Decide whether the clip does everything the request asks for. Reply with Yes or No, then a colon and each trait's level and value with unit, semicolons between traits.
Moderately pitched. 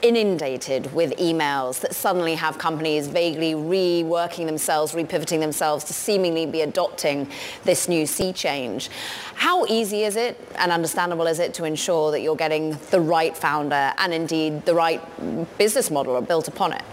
Yes: medium, 165 Hz